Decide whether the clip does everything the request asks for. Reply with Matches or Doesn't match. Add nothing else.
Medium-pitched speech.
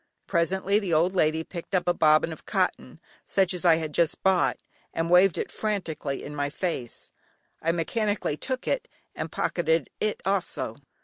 Matches